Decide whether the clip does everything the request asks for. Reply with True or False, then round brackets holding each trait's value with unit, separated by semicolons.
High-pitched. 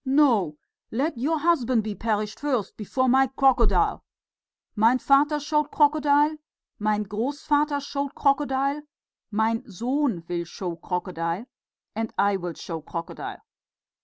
True (245 Hz)